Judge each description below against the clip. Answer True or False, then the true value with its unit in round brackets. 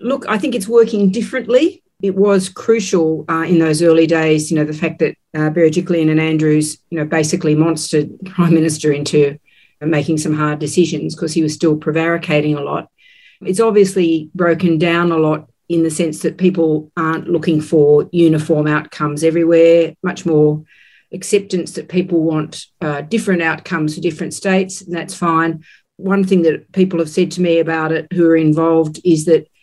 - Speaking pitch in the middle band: True (165 Hz)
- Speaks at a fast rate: False (180 wpm)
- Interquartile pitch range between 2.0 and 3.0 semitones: True (2.5 semitones)